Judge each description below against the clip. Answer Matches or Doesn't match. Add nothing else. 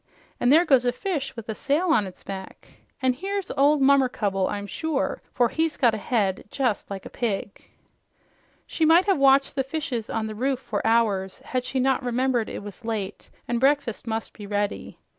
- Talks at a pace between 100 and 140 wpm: Doesn't match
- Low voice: Doesn't match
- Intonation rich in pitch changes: Doesn't match